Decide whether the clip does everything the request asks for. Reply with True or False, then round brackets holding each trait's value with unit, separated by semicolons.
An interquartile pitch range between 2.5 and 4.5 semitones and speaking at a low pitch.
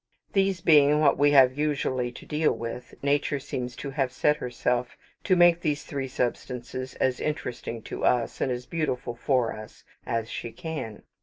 True (3.4 semitones; 130 Hz)